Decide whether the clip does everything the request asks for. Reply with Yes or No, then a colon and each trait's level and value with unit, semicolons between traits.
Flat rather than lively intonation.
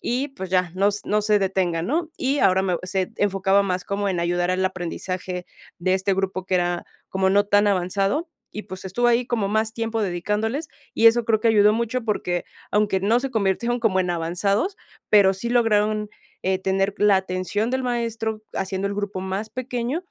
No: average, 3.2 semitones